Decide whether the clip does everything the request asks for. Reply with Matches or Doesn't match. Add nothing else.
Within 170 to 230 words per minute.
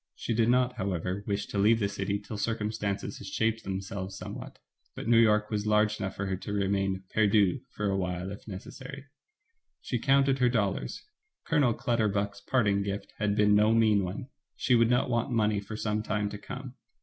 Matches